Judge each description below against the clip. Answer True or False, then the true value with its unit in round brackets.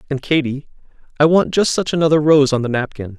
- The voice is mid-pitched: True (145 Hz)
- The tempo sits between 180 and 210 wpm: True (205 wpm)